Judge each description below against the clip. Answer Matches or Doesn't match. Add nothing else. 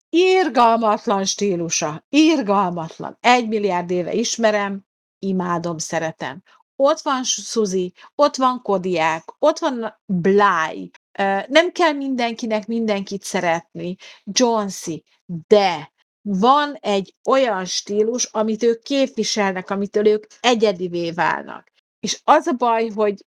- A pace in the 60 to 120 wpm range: Matches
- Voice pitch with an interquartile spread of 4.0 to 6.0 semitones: Matches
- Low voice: Doesn't match